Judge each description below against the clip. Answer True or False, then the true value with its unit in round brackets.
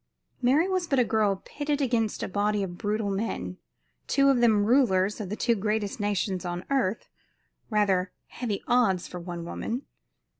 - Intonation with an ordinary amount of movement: True (4.2 semitones)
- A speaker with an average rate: True (165 wpm)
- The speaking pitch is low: False (210 Hz)